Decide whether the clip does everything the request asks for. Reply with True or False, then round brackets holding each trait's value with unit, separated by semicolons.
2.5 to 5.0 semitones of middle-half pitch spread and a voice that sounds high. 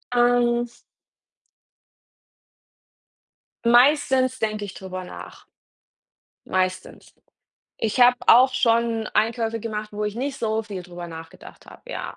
True (2.9 semitones; 225 Hz)